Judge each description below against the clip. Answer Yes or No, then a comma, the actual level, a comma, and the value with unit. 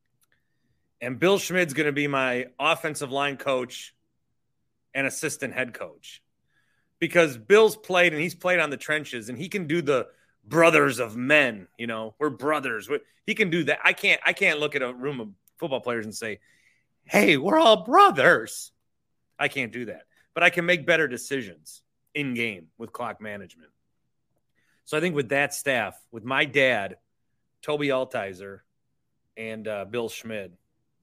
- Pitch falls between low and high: Yes, medium, 145 Hz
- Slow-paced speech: No, average, 165 wpm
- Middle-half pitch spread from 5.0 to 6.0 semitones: Yes, wide, 5.4 semitones